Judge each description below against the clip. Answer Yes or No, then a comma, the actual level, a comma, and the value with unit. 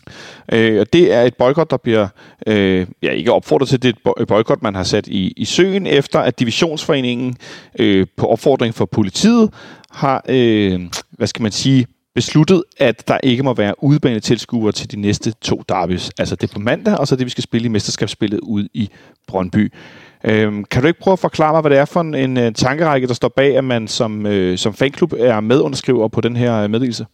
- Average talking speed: Yes, average, 210 wpm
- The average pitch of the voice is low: Yes, low, 120 Hz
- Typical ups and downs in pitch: Yes, average, 4.2 semitones